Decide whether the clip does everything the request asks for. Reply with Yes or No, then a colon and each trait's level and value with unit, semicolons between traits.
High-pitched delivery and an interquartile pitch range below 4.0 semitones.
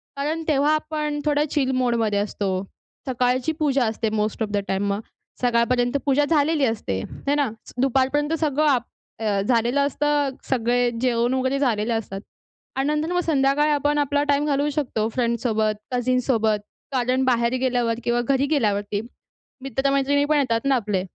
Yes: very high, 260 Hz; average, 3.6 semitones